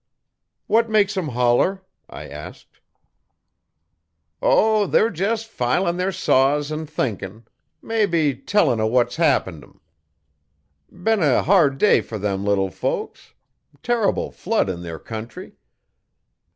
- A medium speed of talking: No, slow, 120 wpm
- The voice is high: No, medium, 150 Hz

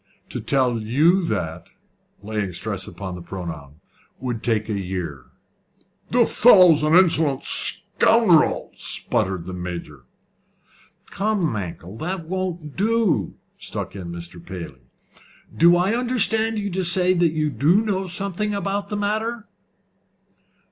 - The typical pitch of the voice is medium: Yes, medium, 155 Hz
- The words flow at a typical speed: No, slow, 130 wpm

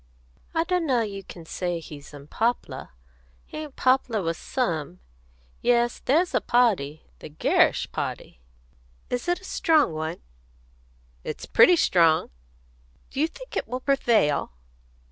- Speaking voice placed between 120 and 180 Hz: No, high, 235 Hz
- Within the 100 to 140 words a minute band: Yes, slow, 135 wpm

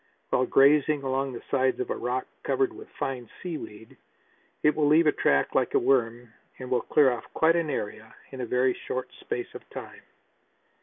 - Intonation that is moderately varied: Yes, average, 3.6 semitones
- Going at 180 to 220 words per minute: Yes, average, 195 wpm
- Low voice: Yes, low, 130 Hz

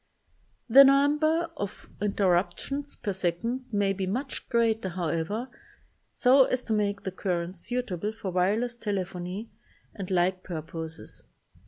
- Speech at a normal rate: No, slow, 130 wpm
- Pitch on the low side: No, high, 205 Hz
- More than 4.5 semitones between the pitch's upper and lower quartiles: Yes, average, 5.2 semitones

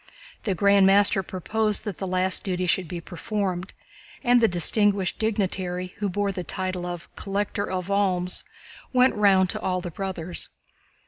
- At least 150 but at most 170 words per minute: Yes, average, 155 wpm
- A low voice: No, high, 190 Hz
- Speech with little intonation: Yes, narrow, 2.0 semitones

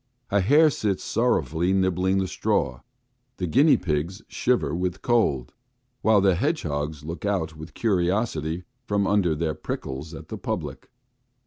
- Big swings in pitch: No, average, 4.4 semitones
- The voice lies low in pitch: Yes, very low, 90 Hz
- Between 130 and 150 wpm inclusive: Yes, average, 140 wpm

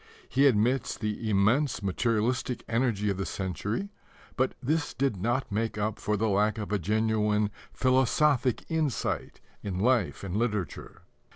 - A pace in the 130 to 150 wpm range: Yes, average, 145 wpm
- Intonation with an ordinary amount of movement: Yes, average, 3.7 semitones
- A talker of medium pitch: No, low, 110 Hz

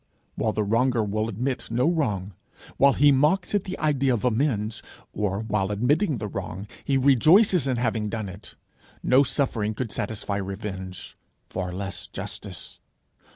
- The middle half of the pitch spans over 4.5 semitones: Yes, average, 5.2 semitones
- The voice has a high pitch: No, low, 110 Hz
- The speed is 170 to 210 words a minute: No, average, 155 wpm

